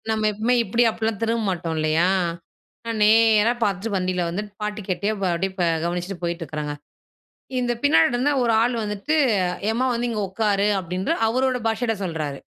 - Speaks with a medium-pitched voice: No, high, 210 Hz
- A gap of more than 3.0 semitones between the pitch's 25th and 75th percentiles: Yes, average, 4.2 semitones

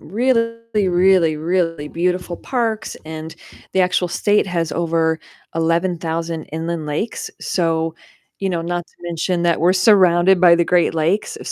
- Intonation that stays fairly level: Yes, narrow, 2.1 semitones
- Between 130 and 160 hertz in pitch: No, medium, 175 Hz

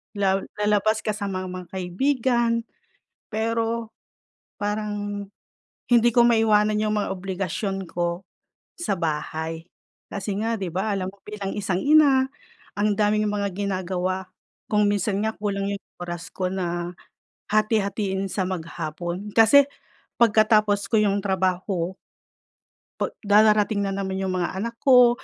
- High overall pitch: Yes, high, 200 Hz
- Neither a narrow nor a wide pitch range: No, narrow, 2.3 semitones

